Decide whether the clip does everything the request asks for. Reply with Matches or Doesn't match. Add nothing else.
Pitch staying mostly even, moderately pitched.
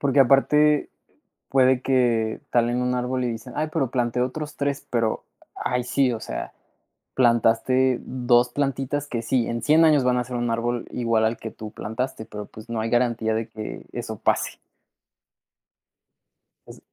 Doesn't match